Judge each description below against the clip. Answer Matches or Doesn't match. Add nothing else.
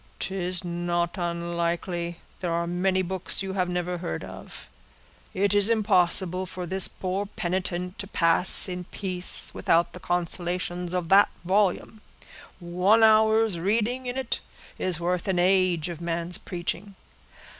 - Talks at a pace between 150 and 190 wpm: Doesn't match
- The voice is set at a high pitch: Doesn't match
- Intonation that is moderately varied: Doesn't match